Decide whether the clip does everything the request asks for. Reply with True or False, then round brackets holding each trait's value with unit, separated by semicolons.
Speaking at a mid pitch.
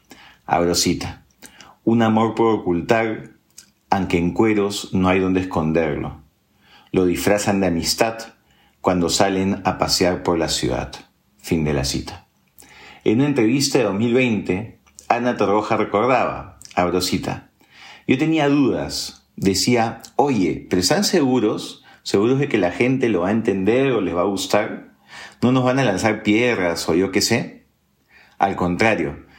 False (100 Hz)